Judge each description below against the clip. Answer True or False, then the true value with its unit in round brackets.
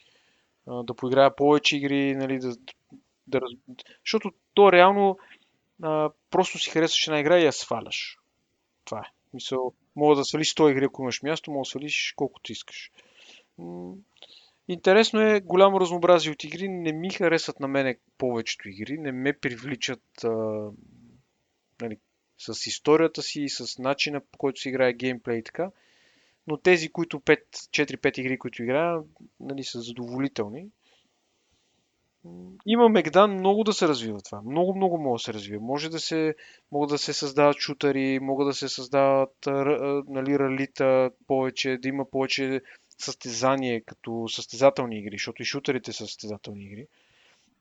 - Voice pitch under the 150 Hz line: True (140 Hz)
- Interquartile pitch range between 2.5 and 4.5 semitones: True (3.7 semitones)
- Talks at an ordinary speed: True (150 wpm)